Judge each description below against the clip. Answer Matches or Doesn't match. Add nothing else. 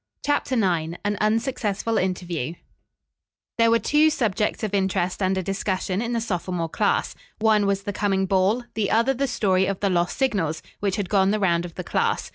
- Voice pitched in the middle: Doesn't match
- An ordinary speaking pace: Matches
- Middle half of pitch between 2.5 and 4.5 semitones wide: Matches